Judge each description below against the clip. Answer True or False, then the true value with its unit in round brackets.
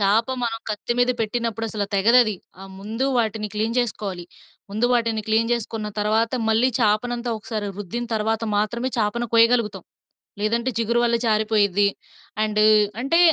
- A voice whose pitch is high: True (220 Hz)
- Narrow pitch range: True (1.9 semitones)